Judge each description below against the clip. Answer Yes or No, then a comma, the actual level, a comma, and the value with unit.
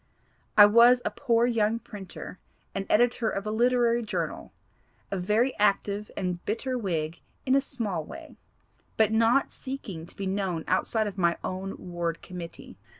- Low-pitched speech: No, high, 210 Hz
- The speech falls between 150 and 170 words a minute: Yes, average, 155 wpm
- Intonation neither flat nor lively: Yes, average, 4.1 semitones